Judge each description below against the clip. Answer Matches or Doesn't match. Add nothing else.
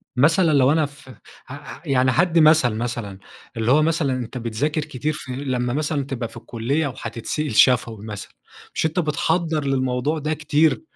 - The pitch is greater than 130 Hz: Matches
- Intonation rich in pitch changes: Doesn't match